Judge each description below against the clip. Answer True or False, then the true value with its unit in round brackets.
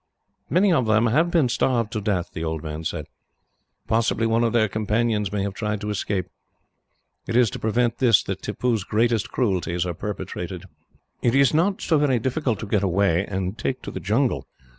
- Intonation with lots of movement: False (3.7 semitones)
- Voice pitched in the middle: False (110 Hz)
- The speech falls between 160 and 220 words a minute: True (190 wpm)